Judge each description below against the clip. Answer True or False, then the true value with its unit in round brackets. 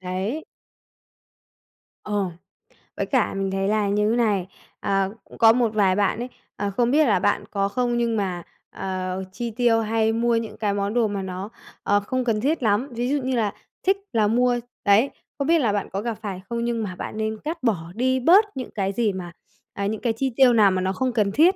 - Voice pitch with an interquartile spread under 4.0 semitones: True (3.4 semitones)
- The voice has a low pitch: False (220 Hz)